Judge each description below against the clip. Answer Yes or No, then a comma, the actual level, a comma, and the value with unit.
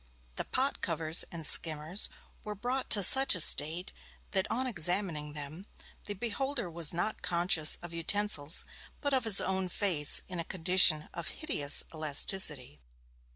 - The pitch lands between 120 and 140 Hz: No, medium, 180 Hz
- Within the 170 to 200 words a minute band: No, average, 150 wpm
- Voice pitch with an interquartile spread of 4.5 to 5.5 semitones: Yes, average, 4.8 semitones